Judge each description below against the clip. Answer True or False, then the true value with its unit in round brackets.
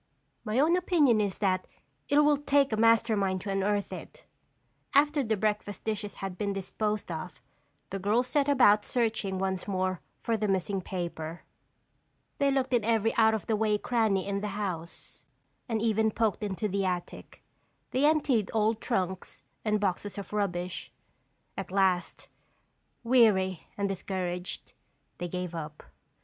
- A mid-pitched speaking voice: False (205 Hz)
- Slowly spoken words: False (155 wpm)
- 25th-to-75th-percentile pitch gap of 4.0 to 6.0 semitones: False (3.3 semitones)